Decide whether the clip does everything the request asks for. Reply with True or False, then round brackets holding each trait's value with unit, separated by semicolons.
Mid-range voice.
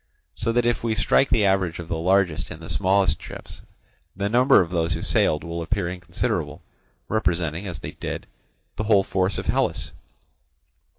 False (95 Hz)